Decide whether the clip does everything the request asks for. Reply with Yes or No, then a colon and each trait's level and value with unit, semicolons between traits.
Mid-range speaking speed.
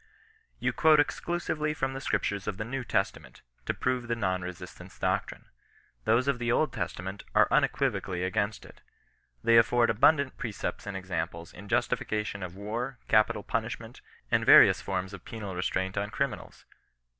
Yes: average, 160 wpm